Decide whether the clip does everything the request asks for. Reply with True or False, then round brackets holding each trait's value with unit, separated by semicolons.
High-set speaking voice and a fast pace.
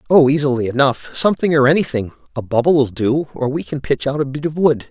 False (140 Hz; 210 wpm)